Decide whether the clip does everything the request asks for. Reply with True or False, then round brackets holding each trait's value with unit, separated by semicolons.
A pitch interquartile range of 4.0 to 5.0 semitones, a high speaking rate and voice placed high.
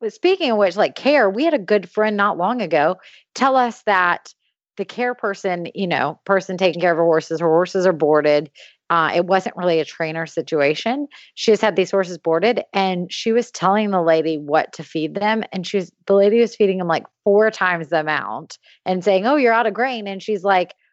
True (4.4 semitones; 220 wpm; 195 Hz)